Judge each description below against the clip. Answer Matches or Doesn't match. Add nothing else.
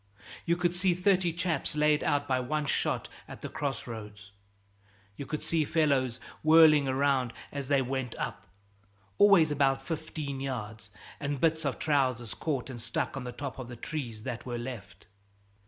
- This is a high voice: Doesn't match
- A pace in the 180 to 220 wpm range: Doesn't match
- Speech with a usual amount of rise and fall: Matches